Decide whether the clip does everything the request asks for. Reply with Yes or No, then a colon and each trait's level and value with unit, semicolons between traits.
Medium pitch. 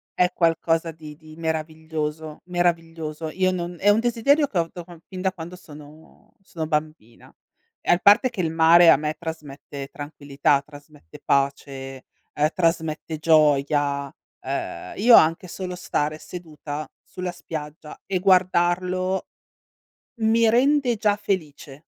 Yes: medium, 165 Hz